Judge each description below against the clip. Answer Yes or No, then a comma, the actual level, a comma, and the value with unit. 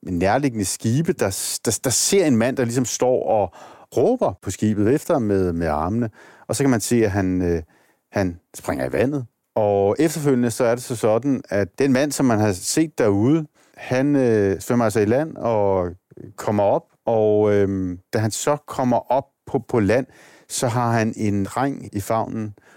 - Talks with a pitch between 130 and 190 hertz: No, low, 110 Hz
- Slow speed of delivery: No, average, 195 wpm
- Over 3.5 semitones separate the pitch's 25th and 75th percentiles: Yes, average, 4.8 semitones